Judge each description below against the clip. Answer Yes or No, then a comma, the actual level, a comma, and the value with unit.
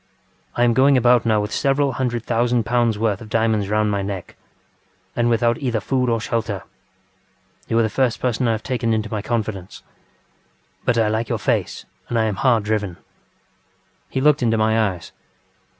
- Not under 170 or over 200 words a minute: Yes, average, 180 wpm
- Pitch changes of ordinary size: No, narrow, 2.1 semitones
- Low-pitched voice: Yes, low, 115 Hz